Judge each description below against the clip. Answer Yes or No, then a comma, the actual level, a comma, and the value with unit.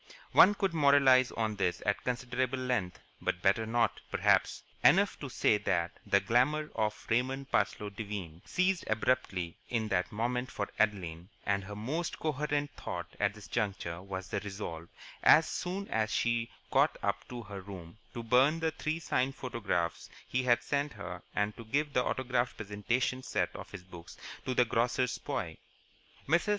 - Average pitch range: Yes, average, 4.6 semitones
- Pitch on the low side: Yes, low, 115 Hz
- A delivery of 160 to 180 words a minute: Yes, average, 165 wpm